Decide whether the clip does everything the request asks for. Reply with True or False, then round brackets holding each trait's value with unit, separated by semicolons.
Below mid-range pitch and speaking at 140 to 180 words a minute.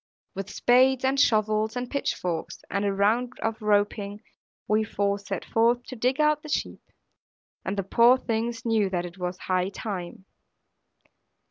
False (215 Hz; 160 wpm)